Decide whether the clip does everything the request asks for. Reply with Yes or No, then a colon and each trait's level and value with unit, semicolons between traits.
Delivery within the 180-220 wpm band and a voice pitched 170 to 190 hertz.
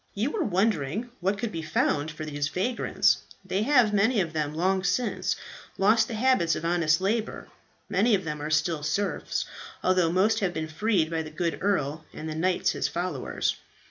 Yes: average, 185 wpm; medium, 185 Hz